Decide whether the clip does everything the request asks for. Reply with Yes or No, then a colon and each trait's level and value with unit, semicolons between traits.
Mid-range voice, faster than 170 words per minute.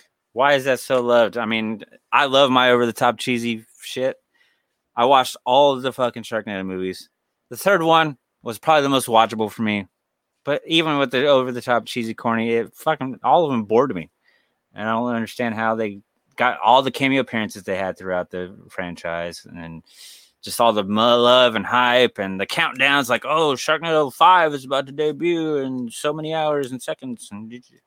No: low, 120 Hz; average, 190 wpm